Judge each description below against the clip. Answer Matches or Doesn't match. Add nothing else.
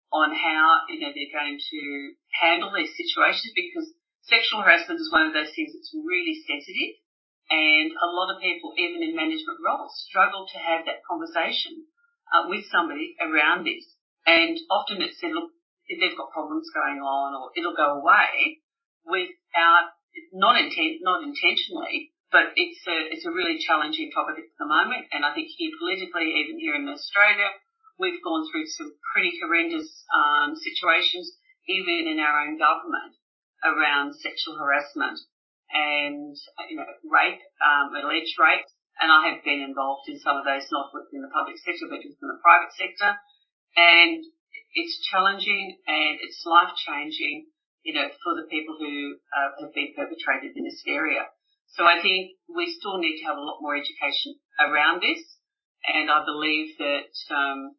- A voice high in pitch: Matches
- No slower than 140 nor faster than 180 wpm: Matches